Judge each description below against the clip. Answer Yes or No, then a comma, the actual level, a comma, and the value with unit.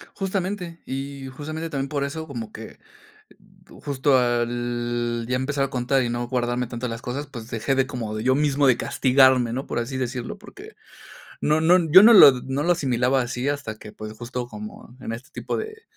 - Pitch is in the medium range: No, low, 130 Hz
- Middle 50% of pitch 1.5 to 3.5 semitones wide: Yes, average, 3.2 semitones